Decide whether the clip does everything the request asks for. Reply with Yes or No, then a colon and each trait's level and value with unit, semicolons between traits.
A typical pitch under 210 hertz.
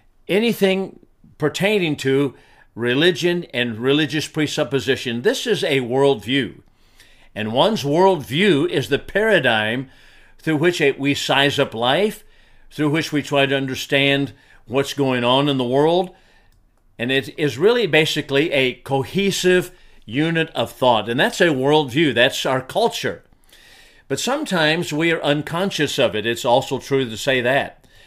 Yes: medium, 140 Hz